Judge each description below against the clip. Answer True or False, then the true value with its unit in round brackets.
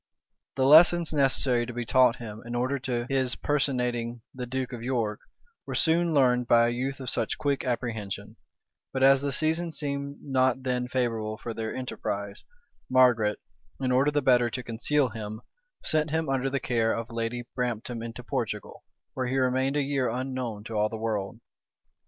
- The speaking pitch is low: True (125 Hz)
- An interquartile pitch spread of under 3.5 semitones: True (2.6 semitones)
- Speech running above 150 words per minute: True (175 wpm)